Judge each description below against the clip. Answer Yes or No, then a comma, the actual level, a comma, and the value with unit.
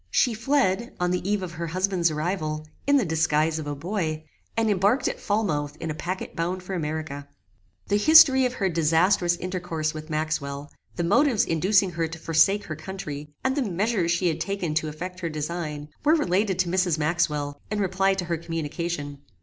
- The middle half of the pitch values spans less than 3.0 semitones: No, average, 3.8 semitones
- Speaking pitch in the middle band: Yes, medium, 175 Hz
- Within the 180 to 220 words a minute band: Yes, average, 190 wpm